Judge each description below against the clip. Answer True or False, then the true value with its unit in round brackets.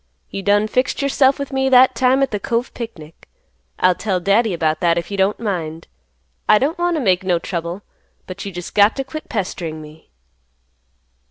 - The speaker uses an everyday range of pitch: False (6.4 semitones)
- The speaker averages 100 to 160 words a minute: False (190 wpm)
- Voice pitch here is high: True (205 Hz)